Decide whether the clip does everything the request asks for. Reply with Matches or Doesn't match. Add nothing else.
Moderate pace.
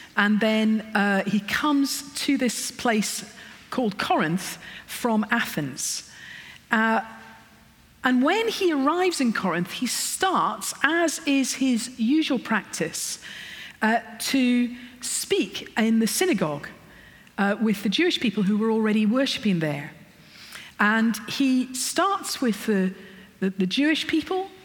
Doesn't match